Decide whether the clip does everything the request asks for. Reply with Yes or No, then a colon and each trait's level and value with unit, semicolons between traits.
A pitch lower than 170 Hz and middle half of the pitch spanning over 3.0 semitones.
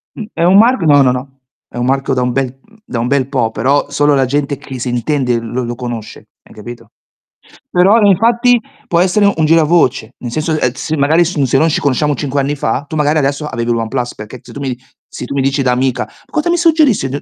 Yes: medium, 140 Hz; average, 4.2 semitones